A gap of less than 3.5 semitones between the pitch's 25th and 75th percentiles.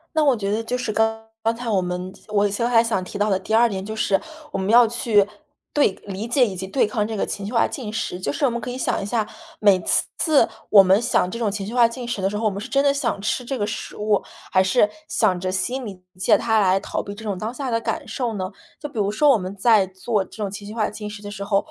Yes: average, 3.1 semitones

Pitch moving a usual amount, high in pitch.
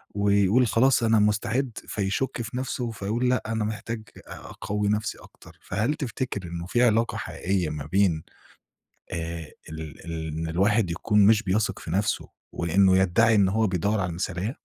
No: average, 3.9 semitones; low, 105 Hz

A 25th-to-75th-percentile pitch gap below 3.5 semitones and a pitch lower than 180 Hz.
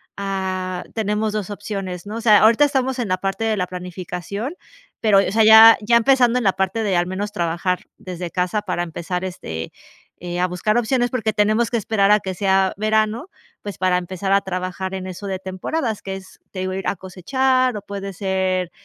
No: average, 2.9 semitones; high, 195 Hz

